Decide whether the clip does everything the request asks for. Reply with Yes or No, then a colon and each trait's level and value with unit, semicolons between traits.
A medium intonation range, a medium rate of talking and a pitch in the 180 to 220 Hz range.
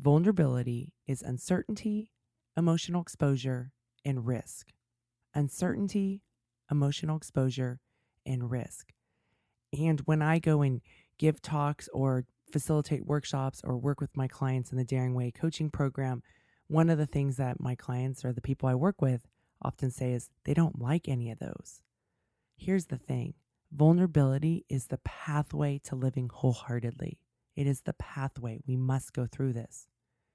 No: average, 3.6 semitones; average, 145 wpm; low, 135 Hz